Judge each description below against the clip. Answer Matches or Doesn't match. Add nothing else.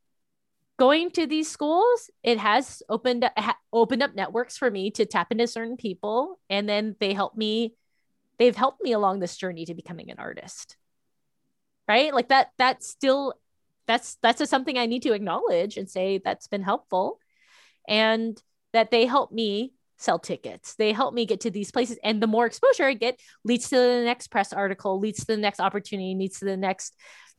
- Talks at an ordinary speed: Matches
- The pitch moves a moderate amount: Matches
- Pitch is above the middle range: Matches